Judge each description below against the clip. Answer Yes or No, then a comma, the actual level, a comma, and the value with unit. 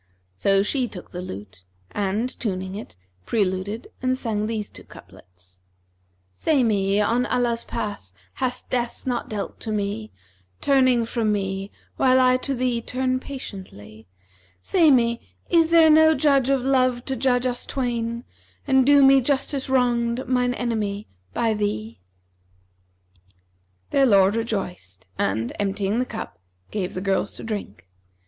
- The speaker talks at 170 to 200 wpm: No, average, 145 wpm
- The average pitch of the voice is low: No, high, 230 Hz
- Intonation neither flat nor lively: Yes, average, 4.6 semitones